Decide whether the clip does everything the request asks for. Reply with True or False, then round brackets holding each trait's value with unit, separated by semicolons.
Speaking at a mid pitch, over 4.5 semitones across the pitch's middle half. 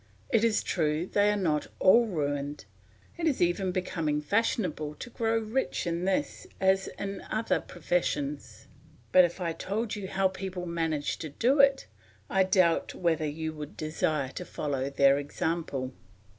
True (180 Hz; 5.2 semitones)